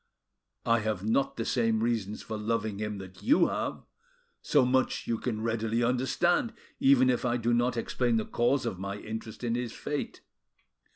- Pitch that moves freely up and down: No, narrow, 2.4 semitones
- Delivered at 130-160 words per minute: No, average, 175 wpm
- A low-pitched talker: Yes, low, 115 Hz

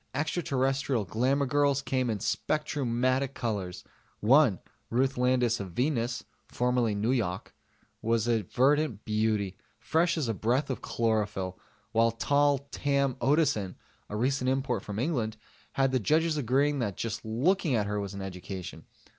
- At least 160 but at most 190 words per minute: No, average, 140 wpm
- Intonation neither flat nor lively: Yes, average, 4.3 semitones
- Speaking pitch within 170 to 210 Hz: No, low, 125 Hz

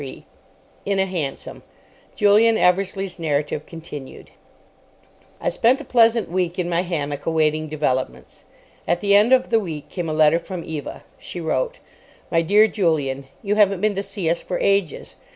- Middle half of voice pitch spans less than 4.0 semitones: No, average, 4.5 semitones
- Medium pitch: Yes, medium, 175 Hz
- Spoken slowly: No, average, 165 wpm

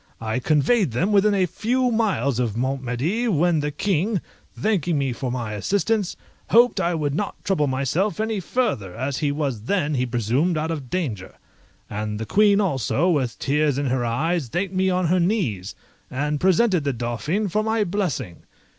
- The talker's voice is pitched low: No, medium, 155 Hz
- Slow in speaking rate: No, average, 180 wpm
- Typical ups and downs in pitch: No, wide, 7.4 semitones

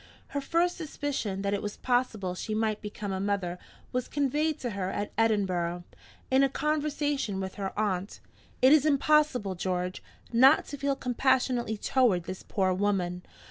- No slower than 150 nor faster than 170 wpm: Yes, average, 160 wpm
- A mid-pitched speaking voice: No, high, 215 Hz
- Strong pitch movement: Yes, wide, 6.2 semitones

